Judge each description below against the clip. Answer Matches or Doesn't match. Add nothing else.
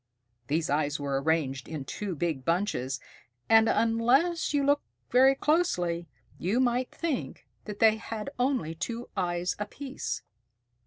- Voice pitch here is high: Matches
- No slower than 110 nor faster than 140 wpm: Matches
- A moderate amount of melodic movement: Doesn't match